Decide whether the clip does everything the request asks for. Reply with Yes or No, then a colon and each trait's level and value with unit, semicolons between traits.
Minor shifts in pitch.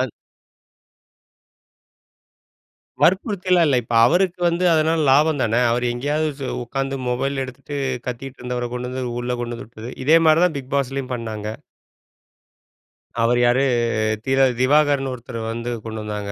No: average, 3.7 semitones